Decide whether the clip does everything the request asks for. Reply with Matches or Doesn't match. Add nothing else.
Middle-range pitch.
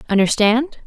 Doesn't match